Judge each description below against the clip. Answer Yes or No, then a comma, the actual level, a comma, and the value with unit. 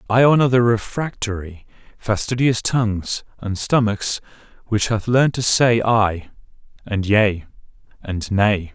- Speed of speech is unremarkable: No, slow, 125 wpm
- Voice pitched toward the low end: Yes, low, 110 Hz